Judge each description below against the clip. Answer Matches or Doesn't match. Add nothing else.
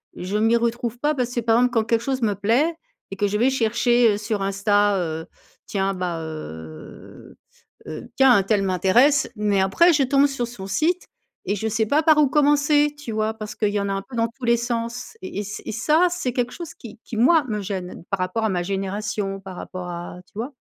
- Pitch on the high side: Matches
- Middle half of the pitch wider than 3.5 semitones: Matches